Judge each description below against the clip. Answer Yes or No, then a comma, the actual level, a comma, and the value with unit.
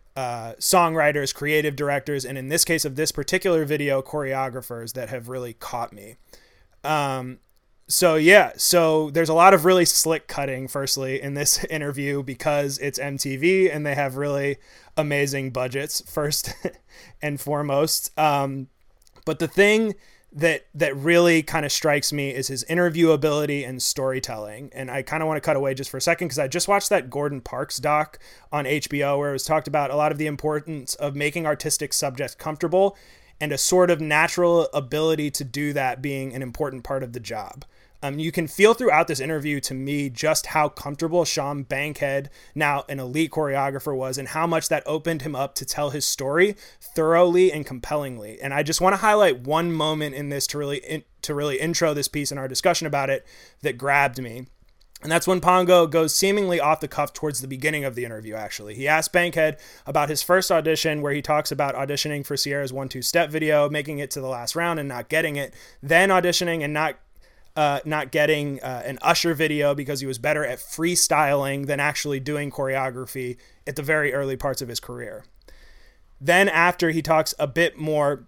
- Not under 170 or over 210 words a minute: Yes, average, 195 wpm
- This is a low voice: No, medium, 150 Hz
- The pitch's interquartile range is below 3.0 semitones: Yes, narrow, 2.5 semitones